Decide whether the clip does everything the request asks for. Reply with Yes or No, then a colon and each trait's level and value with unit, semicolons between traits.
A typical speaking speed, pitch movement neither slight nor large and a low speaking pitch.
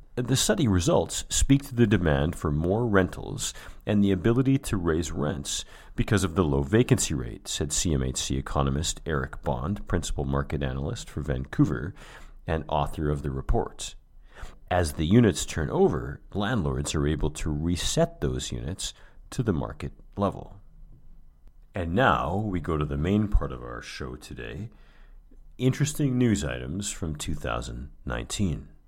No: average, 145 wpm; wide, 6.1 semitones; very low, 80 Hz